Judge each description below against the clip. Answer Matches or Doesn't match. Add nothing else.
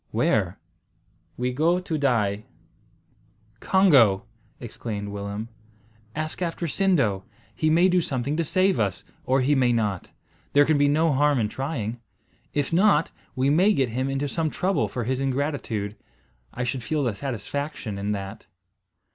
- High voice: Doesn't match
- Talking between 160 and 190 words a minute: Doesn't match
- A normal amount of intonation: Doesn't match